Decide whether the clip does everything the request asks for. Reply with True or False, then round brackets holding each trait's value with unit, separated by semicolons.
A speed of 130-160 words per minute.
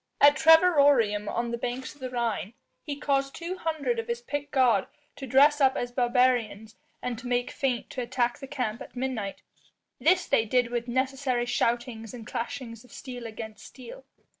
False (180 wpm)